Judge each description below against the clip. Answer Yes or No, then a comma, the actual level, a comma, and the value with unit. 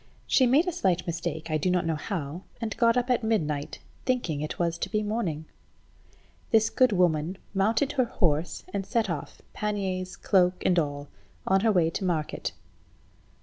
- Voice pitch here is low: No, medium, 185 Hz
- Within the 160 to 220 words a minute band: Yes, average, 170 wpm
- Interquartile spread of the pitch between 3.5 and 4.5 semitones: No, average, 5.3 semitones